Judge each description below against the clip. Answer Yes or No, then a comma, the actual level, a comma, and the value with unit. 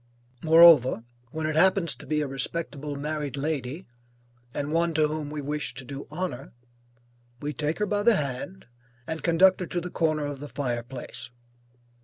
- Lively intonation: No, average, 3.0 semitones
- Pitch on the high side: No, medium, 150 Hz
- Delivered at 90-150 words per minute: No, average, 175 wpm